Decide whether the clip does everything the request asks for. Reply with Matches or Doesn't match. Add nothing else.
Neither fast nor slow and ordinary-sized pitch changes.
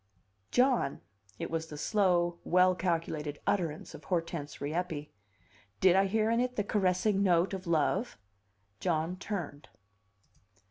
Doesn't match